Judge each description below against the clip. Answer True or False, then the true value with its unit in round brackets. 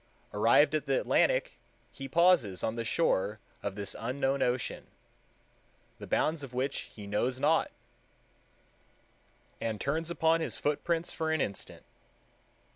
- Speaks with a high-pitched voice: False (135 Hz)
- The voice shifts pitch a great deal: True (6.5 semitones)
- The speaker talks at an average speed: False (130 wpm)